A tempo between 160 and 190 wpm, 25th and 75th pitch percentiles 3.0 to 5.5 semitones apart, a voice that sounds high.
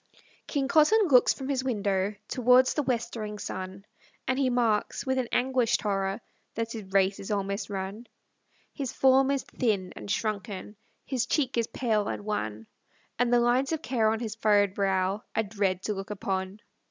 Yes: average, 175 wpm; average, 4.3 semitones; high, 220 Hz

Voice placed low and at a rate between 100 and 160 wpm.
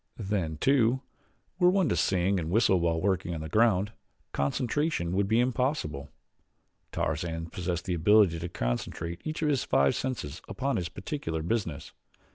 Yes: very low, 95 Hz; average, 155 wpm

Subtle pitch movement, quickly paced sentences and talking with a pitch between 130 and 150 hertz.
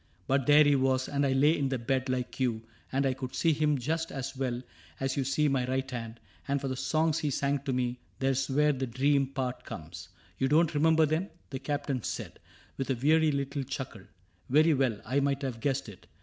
Yes: narrow, 2.1 semitones; fast, 235 wpm; low, 135 Hz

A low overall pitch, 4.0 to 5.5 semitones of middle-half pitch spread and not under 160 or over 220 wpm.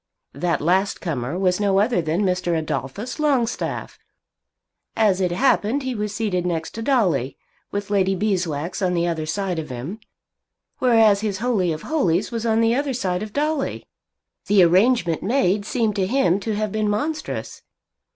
No: high, 200 Hz; average, 4.4 semitones; average, 165 wpm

